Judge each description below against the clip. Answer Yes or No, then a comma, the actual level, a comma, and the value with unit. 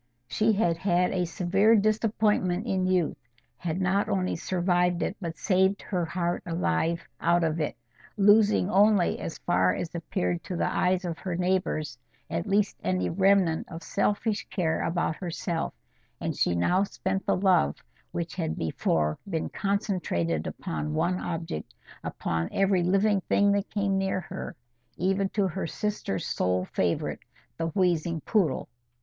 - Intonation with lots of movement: No, average, 3.3 semitones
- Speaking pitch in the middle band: Yes, medium, 180 Hz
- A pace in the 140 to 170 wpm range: Yes, average, 150 wpm